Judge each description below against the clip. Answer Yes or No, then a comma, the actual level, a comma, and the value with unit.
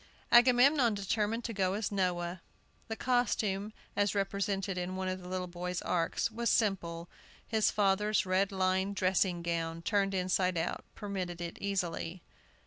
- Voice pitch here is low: No, high, 190 Hz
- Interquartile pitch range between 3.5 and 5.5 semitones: No, narrow, 2.5 semitones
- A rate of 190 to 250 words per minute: No, average, 145 wpm